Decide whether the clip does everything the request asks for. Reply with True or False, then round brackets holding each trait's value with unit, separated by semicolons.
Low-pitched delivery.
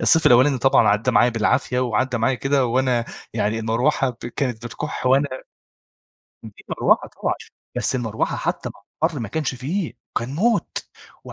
True (125 Hz)